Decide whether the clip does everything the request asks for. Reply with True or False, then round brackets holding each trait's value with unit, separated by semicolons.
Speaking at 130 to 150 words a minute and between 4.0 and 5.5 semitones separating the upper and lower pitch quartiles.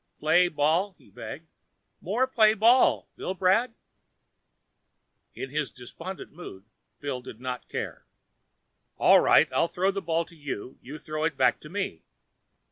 True (145 wpm; 5.1 semitones)